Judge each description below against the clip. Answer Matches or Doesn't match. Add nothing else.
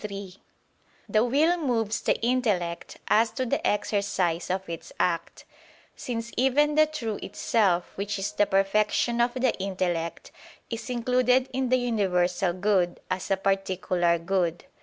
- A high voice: Matches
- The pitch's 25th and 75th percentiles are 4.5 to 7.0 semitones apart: Matches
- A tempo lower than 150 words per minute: Matches